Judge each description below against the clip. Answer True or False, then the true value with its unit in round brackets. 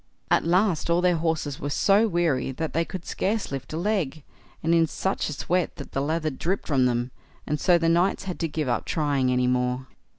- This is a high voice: False (160 Hz)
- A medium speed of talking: False (220 wpm)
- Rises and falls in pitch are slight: False (4.4 semitones)